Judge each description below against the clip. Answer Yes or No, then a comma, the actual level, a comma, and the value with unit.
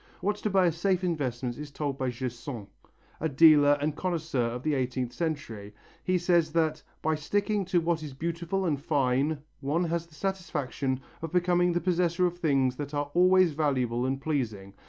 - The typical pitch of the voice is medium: Yes, medium, 155 Hz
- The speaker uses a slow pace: No, average, 180 wpm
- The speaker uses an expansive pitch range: No, average, 4.6 semitones